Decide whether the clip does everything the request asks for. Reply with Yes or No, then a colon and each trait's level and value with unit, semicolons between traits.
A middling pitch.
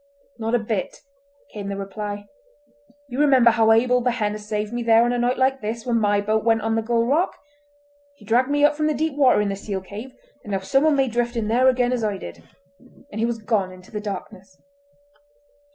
No: high, 225 Hz